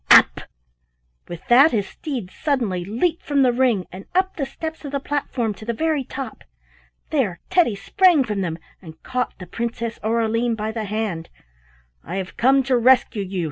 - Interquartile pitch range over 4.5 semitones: Yes, wide, 5.4 semitones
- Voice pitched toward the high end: Yes, high, 235 Hz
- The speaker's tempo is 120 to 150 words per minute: No, average, 180 wpm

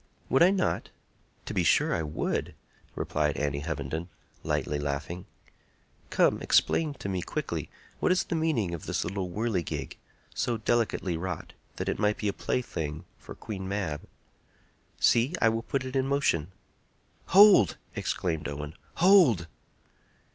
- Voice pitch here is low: Yes, low, 100 Hz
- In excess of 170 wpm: No, average, 145 wpm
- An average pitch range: No, wide, 8.3 semitones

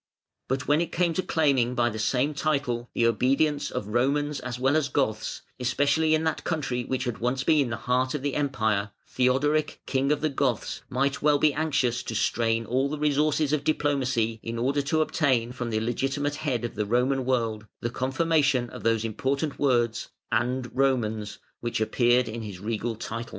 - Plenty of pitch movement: No, average, 3.6 semitones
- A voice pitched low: Yes, low, 130 Hz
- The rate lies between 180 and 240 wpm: Yes, average, 185 wpm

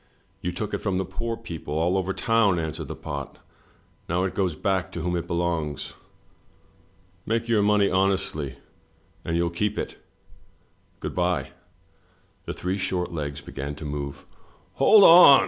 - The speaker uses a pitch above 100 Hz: No, very low, 90 Hz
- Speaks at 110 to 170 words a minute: Yes, average, 160 wpm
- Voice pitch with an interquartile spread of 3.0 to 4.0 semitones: Yes, average, 3.6 semitones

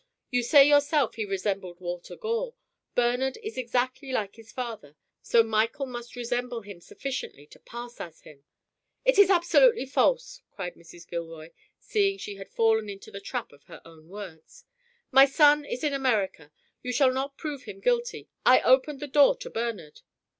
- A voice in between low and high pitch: No, high, 245 Hz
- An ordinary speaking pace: Yes, average, 170 wpm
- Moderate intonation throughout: No, wide, 6.5 semitones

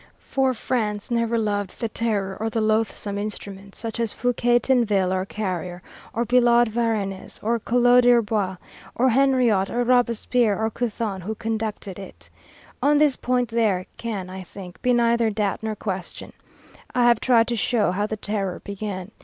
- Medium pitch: No, high, 220 Hz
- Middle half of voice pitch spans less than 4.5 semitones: Yes, average, 3.1 semitones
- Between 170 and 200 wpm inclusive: No, average, 160 wpm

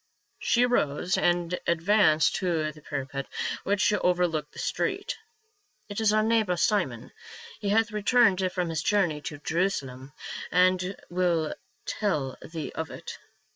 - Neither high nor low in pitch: Yes, medium, 180 Hz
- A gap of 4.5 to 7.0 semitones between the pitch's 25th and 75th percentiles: Yes, average, 4.9 semitones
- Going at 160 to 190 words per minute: No, average, 140 wpm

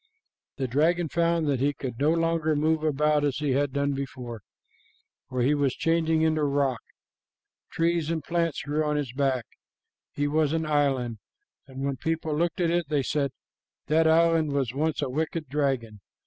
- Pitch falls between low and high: Yes, medium, 150 Hz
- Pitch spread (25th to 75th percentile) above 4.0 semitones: No, average, 2.8 semitones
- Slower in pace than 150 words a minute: No, average, 170 wpm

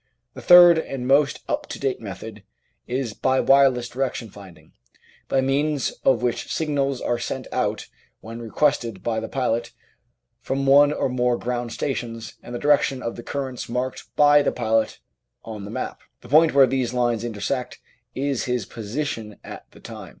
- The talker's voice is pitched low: Yes, low, 125 Hz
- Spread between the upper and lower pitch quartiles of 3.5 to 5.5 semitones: No, average, 2.9 semitones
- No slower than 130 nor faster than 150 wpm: No, average, 170 wpm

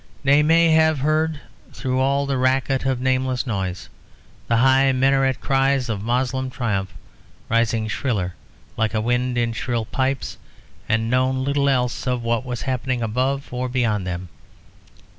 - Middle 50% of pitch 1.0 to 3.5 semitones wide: Yes, narrow, 2.6 semitones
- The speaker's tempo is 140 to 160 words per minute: Yes, average, 150 wpm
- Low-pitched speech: Yes, low, 130 Hz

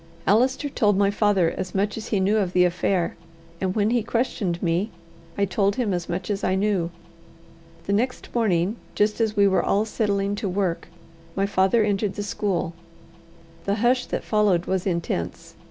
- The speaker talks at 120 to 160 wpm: No, average, 180 wpm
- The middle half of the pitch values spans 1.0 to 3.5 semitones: Yes, narrow, 2.4 semitones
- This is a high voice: Yes, high, 200 Hz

